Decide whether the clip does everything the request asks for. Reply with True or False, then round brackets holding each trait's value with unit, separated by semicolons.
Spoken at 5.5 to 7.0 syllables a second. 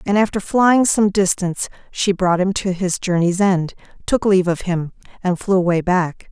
False (4.9 syllables/s)